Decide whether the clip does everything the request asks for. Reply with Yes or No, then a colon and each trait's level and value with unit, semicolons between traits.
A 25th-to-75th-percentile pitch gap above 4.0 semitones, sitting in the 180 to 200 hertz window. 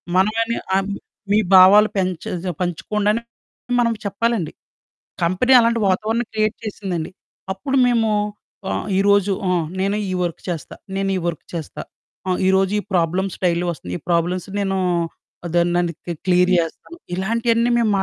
No: average, 3.6 semitones; high, 190 Hz